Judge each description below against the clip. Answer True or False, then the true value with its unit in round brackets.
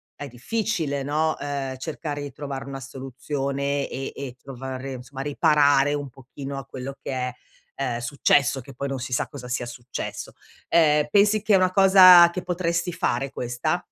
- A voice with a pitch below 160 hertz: True (140 Hz)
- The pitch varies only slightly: False (3.1 semitones)